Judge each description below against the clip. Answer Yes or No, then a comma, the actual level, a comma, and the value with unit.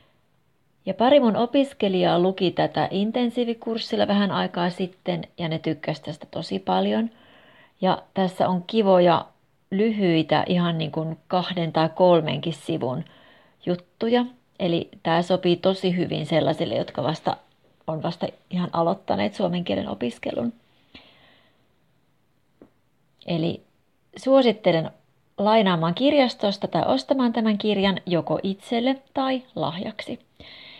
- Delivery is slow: No, average, 110 wpm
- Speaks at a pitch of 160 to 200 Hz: Yes, medium, 185 Hz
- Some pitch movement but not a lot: Yes, average, 4.7 semitones